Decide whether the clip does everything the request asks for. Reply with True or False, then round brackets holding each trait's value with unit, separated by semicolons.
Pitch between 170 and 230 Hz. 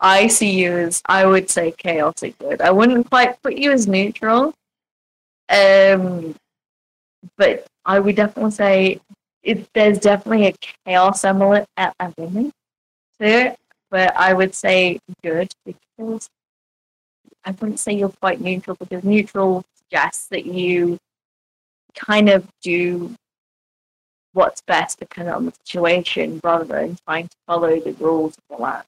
True (190 Hz)